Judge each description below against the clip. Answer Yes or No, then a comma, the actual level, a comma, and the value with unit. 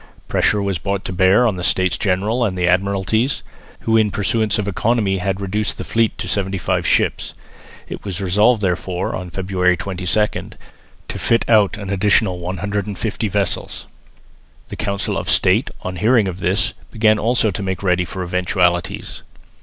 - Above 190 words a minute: No, average, 165 wpm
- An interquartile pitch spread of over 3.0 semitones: No, narrow, 2.6 semitones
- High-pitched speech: No, low, 100 Hz